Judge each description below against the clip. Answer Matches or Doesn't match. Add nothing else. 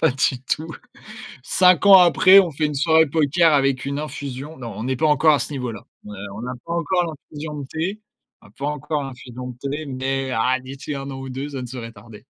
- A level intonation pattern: Doesn't match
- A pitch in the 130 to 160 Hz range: Matches